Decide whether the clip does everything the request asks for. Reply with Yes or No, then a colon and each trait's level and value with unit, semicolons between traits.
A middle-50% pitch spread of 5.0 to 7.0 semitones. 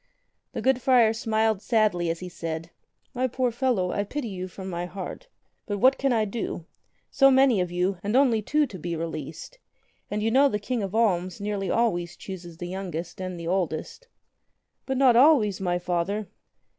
Yes: average, 5.3 semitones